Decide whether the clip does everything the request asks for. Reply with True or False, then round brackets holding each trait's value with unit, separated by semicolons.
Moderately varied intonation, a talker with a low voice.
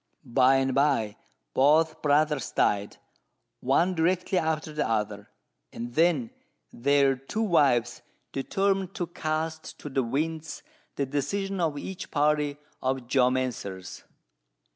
False (3.9 semitones; 145 Hz)